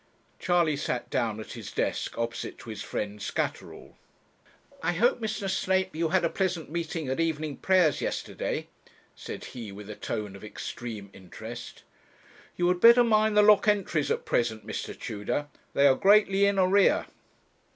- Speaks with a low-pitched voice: No, medium, 160 Hz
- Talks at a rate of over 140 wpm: Yes, average, 160 wpm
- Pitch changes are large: Yes, wide, 8.6 semitones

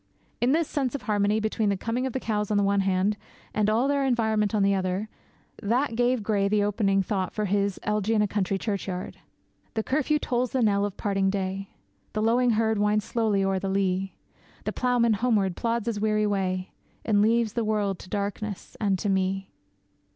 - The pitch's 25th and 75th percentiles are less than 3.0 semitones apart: Yes, narrow, 2.6 semitones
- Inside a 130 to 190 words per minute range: No, average, 200 wpm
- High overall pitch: Yes, high, 210 Hz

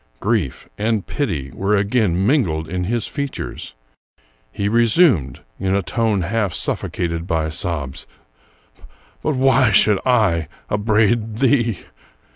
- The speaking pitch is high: No, low, 105 Hz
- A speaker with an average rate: No, slow, 125 wpm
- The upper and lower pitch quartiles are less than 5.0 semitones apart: No, wide, 5.6 semitones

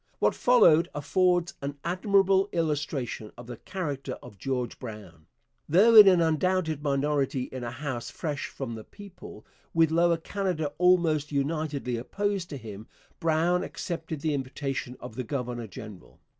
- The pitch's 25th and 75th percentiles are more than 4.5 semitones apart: Yes, wide, 5.6 semitones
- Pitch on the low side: No, medium, 150 Hz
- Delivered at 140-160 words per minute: Yes, average, 145 wpm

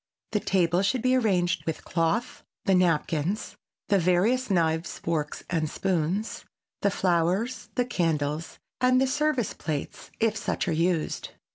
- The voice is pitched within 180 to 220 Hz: Yes, medium, 185 Hz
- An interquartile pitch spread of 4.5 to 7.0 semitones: Yes, average, 5.2 semitones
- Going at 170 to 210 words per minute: No, average, 140 wpm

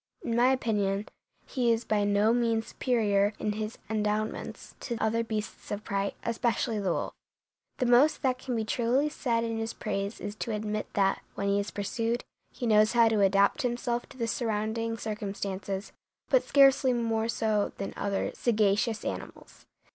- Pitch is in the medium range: No, high, 220 Hz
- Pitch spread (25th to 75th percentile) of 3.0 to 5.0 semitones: No, narrow, 2.4 semitones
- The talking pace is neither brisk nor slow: Yes, average, 170 wpm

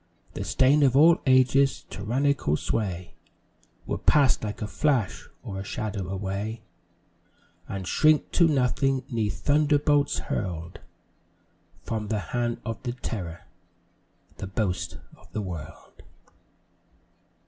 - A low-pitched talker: Yes, low, 115 Hz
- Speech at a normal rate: No, slow, 115 wpm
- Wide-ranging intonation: Yes, wide, 5.9 semitones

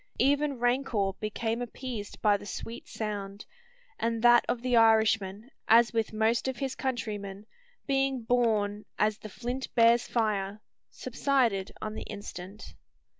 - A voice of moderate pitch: No, high, 225 Hz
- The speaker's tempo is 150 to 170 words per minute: No, slow, 135 wpm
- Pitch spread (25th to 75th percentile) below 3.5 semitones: Yes, average, 2.8 semitones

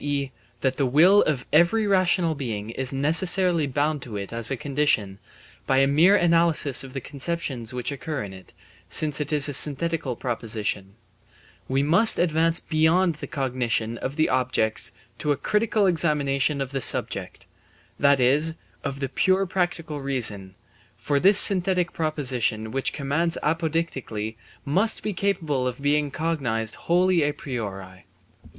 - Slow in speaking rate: No, average, 150 wpm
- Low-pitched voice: No, medium, 145 Hz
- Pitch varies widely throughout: No, average, 4.7 semitones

